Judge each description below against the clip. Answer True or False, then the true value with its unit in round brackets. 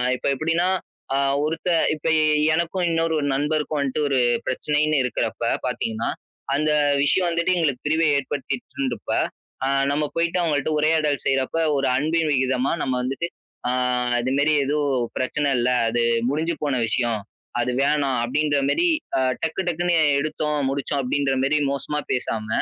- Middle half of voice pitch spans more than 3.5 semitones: False (2.9 semitones)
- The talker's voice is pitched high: False (145 Hz)